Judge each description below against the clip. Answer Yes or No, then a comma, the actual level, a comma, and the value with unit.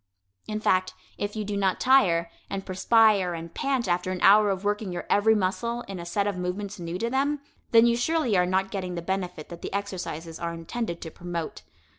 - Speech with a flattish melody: No, average, 3.3 semitones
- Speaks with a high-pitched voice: Yes, high, 195 Hz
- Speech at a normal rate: No, fast, 210 wpm